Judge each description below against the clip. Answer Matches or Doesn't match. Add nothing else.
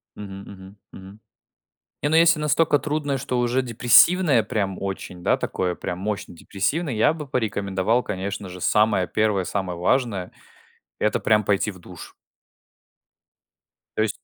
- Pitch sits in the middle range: Doesn't match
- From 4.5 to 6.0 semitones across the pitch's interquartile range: Matches